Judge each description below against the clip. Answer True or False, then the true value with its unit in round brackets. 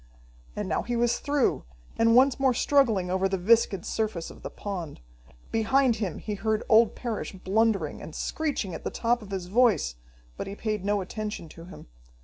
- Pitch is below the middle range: False (215 Hz)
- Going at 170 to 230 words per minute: True (185 wpm)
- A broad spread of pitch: False (3.7 semitones)